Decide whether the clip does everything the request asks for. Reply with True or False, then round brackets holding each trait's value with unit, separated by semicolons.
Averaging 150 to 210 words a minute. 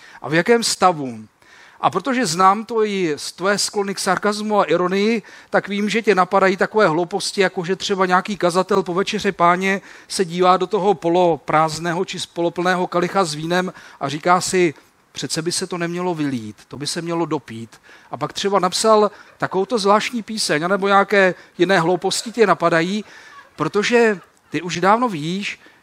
True (170 wpm)